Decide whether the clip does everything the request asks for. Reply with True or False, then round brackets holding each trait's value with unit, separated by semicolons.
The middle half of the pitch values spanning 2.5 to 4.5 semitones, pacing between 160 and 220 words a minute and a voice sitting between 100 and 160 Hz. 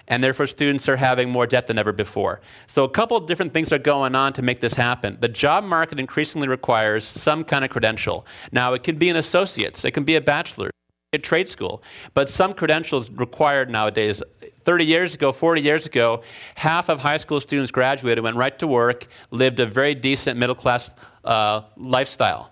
True (3.9 semitones; 200 wpm; 135 Hz)